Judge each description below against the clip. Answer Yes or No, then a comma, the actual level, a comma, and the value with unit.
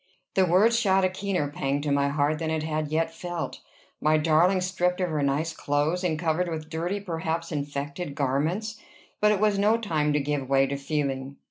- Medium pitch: Yes, medium, 160 Hz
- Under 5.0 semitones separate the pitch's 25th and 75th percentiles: Yes, average, 3.8 semitones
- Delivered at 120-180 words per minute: No, average, 200 wpm